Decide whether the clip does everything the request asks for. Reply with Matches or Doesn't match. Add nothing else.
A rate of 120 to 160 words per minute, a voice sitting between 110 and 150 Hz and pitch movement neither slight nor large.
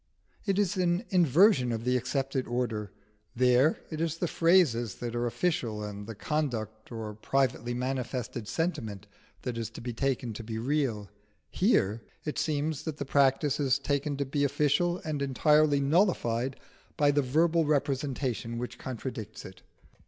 Matches